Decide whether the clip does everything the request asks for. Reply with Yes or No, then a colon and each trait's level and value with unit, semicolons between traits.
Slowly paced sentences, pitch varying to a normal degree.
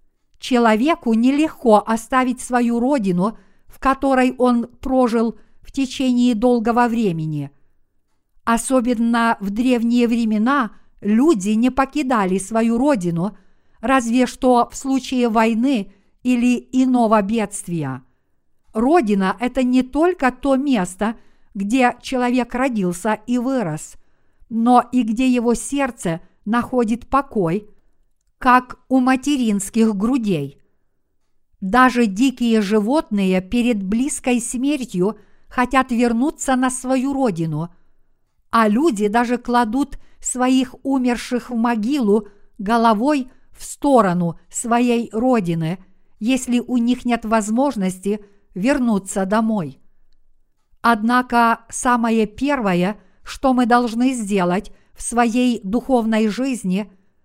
Yes: slow, 100 wpm; average, 3.3 semitones